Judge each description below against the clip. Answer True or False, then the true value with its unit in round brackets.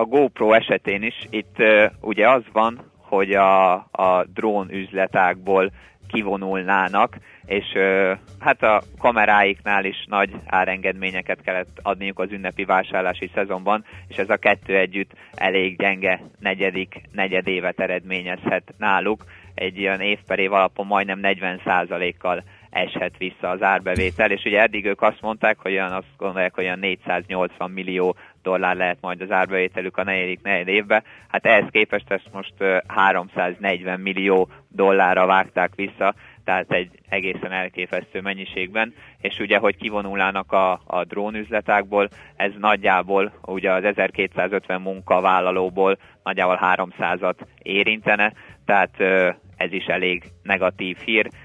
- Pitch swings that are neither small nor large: False (1.6 semitones)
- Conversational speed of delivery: True (130 wpm)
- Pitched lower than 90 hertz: False (95 Hz)